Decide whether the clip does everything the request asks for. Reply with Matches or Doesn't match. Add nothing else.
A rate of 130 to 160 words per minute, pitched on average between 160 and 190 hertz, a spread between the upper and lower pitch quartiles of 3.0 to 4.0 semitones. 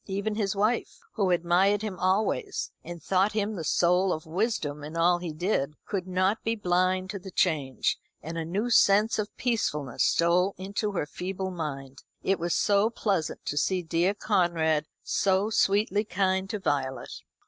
Doesn't match